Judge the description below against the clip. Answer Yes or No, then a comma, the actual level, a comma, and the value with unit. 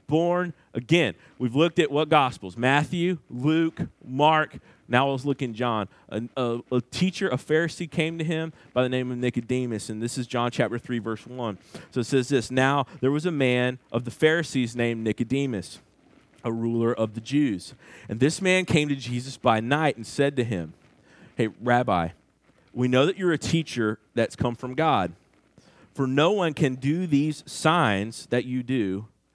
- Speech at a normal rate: Yes, average, 185 wpm